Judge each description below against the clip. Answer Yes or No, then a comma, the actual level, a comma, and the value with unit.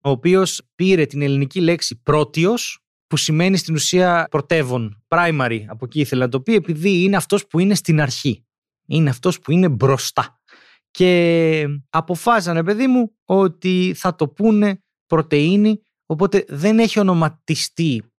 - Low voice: No, medium, 165 Hz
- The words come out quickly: No, average, 145 wpm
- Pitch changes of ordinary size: Yes, average, 4.4 semitones